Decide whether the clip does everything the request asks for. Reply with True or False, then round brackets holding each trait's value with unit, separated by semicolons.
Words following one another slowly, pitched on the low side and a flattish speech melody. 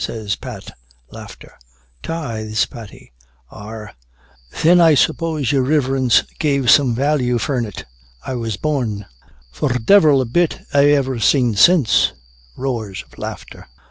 False (125 wpm; 130 Hz; 4.6 semitones)